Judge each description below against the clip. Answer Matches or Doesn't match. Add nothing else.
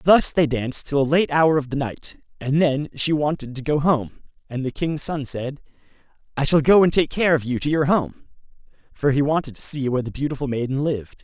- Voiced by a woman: Doesn't match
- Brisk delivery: Matches